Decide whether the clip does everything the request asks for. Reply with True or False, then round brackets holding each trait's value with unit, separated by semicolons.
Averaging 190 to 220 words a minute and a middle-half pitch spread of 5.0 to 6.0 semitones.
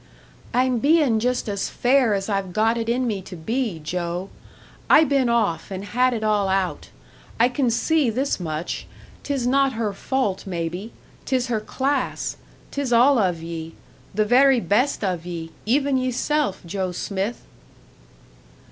False (155 wpm; 5.3 semitones)